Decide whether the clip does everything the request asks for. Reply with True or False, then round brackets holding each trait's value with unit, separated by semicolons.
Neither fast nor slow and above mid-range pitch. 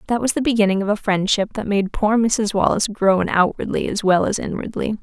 False (215 wpm; 210 Hz)